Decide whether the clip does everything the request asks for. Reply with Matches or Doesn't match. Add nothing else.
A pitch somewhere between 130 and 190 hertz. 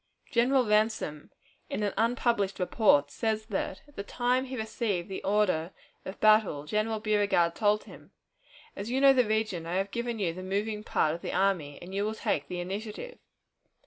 Doesn't match